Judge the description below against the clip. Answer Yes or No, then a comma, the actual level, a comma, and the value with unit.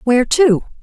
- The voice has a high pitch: Yes, very high, 260 Hz